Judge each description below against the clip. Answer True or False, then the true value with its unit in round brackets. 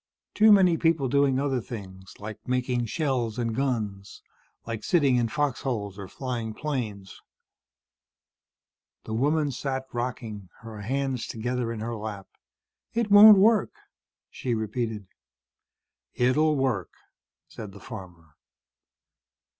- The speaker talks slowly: True (120 wpm)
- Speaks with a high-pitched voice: False (120 Hz)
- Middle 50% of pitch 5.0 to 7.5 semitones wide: False (4.4 semitones)